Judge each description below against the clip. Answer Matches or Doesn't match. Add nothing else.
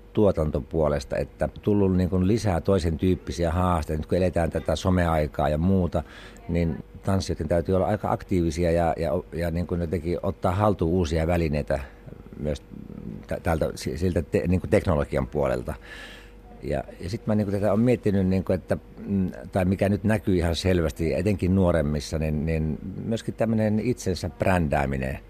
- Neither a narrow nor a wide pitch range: Matches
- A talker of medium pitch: Doesn't match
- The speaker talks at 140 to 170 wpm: Matches